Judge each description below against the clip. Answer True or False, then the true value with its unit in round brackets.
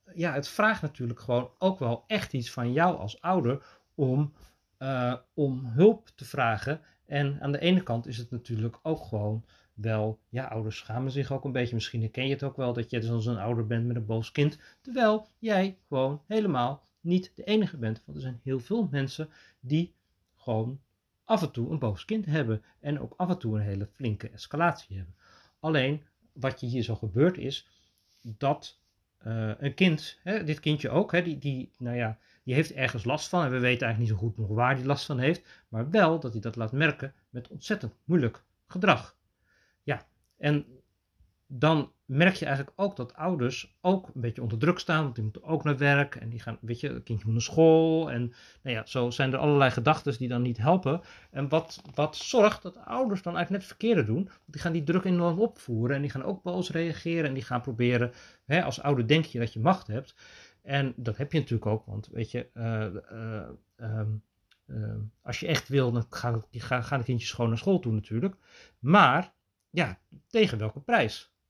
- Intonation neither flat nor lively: False (5.8 semitones)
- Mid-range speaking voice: False (130 Hz)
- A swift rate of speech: True (210 wpm)